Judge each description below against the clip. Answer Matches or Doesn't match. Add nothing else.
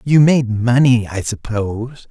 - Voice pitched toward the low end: Matches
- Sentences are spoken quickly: Doesn't match